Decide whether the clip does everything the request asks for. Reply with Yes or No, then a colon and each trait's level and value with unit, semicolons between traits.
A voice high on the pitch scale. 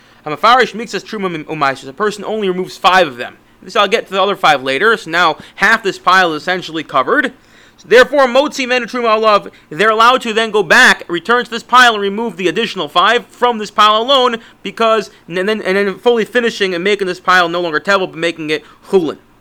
Yes: high, 205 Hz